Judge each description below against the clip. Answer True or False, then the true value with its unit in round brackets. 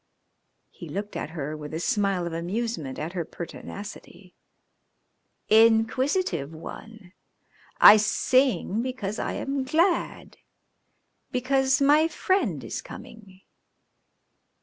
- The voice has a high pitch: True (215 Hz)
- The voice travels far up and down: True (7.0 semitones)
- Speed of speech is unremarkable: False (105 wpm)